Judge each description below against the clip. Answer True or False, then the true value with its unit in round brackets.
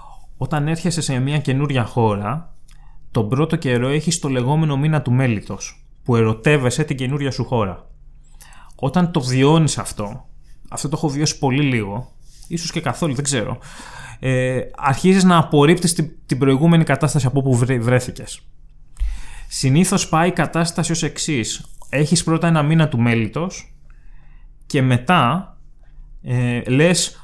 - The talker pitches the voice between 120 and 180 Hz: True (140 Hz)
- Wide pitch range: False (4.2 semitones)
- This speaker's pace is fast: False (140 wpm)